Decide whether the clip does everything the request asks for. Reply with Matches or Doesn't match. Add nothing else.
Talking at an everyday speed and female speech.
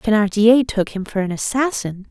Matches